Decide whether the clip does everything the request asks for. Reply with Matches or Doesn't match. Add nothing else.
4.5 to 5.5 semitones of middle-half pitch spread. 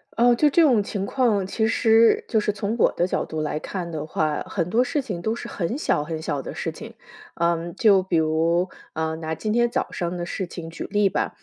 Matches